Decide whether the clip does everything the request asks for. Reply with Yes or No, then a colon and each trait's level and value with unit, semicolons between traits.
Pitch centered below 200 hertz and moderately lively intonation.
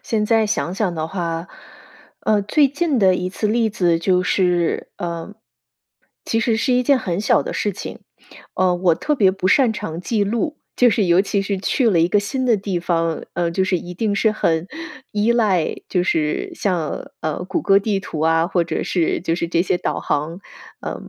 Yes: high, 190 Hz; average, 4.0 semitones